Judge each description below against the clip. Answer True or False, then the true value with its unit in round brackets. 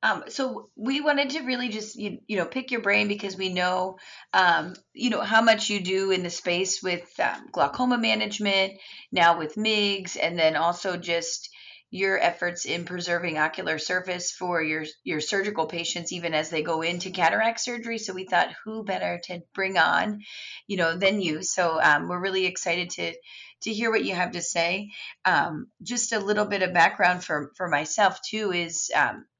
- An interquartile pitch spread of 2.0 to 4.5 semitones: True (3.6 semitones)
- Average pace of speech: True (190 wpm)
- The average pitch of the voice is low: False (185 Hz)